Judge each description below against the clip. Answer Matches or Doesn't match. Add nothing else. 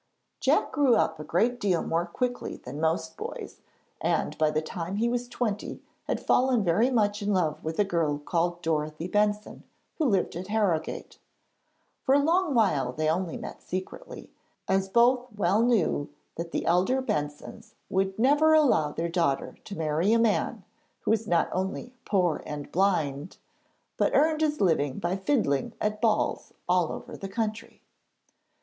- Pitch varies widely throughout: Matches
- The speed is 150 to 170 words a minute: Matches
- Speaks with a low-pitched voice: Doesn't match